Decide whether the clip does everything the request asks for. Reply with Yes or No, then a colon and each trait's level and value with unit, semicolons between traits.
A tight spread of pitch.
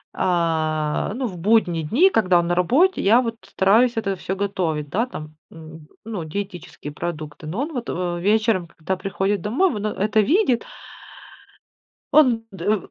No: average, 5.1 semitones